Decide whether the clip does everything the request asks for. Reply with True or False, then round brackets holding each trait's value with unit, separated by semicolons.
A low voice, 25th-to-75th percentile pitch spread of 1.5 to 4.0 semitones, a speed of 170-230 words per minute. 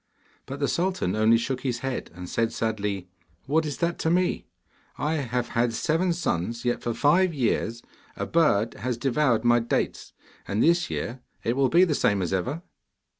False (125 Hz; 5.6 semitones; 180 wpm)